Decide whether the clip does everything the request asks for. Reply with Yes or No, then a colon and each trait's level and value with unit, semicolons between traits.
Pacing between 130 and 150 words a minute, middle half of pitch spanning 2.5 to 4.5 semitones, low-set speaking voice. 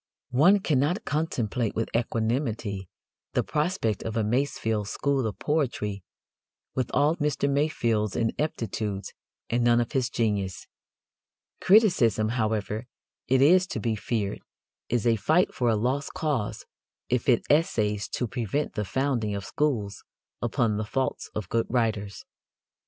No: slow, 135 wpm; average, 4.9 semitones; low, 120 Hz